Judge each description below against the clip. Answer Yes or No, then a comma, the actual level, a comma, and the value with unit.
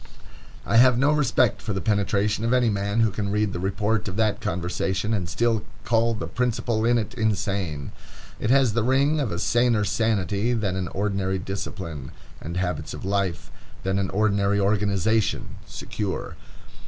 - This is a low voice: Yes, low, 105 Hz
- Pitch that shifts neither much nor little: Yes, average, 3.0 semitones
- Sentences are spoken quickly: No, average, 165 wpm